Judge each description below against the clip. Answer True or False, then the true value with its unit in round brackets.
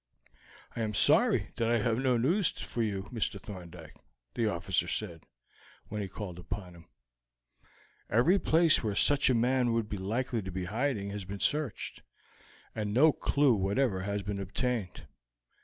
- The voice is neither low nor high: False (105 Hz)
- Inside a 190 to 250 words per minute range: False (165 wpm)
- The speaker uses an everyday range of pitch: True (4.4 semitones)